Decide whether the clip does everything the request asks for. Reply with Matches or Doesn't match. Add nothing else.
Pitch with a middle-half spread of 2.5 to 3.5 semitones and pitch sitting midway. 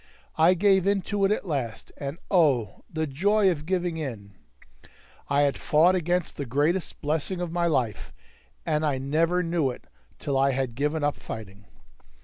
Doesn't match